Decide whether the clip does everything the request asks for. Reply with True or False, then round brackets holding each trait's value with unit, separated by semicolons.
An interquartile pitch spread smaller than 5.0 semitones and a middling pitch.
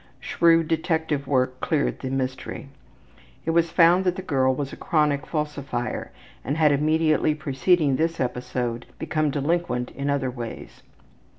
True (3.7 semitones; 150 Hz)